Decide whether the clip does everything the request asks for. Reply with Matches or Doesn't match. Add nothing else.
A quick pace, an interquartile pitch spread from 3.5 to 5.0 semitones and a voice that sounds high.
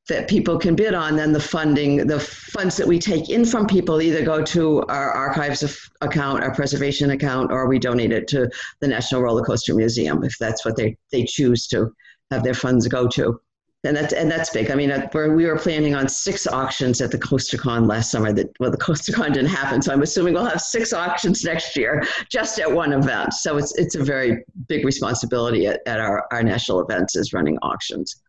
Doesn't match